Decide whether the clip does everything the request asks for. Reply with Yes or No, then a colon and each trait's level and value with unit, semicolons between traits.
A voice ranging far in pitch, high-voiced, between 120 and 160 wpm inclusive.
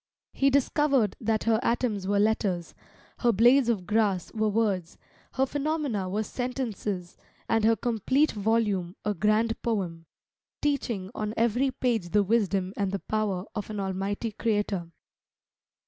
No: average, 3.2 semitones; high, 215 Hz; average, 140 wpm